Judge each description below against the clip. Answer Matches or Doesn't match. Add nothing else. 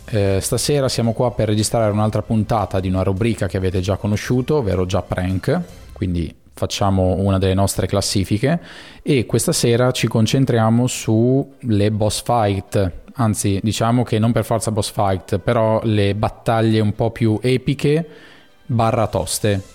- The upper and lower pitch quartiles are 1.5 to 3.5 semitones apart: Matches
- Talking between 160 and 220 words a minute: Doesn't match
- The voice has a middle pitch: Doesn't match